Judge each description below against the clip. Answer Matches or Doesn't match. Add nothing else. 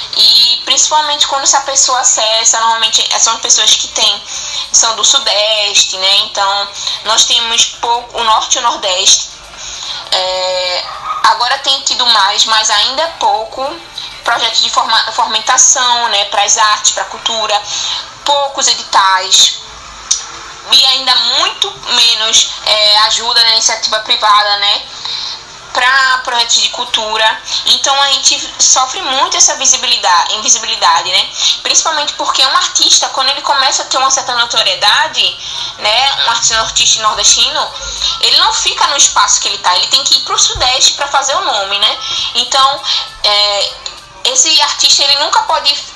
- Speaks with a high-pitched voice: Matches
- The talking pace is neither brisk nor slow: Matches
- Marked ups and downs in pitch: Doesn't match